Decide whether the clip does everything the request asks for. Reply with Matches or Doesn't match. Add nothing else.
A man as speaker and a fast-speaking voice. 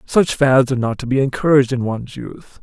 Matches